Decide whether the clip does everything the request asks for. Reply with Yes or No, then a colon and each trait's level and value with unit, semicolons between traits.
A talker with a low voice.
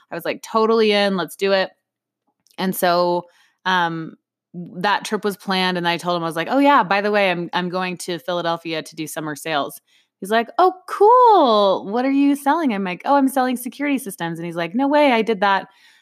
No: high, 195 Hz